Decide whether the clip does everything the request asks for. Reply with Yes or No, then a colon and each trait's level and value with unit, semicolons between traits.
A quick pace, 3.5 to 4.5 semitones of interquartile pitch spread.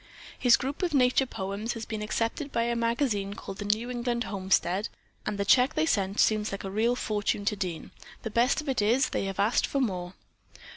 Yes: fast, 210 wpm; average, 3.8 semitones